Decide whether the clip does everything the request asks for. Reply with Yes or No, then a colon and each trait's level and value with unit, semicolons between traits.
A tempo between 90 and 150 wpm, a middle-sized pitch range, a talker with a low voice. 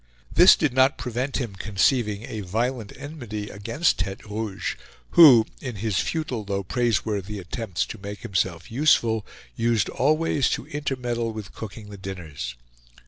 Yes: average, 140 wpm; average, 4.1 semitones; low, 110 Hz